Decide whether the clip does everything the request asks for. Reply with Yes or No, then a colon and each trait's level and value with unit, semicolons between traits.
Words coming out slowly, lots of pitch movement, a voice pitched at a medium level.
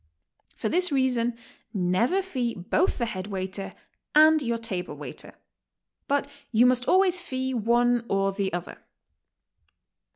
No: slow, 130 wpm; wide, 5.8 semitones; high, 240 Hz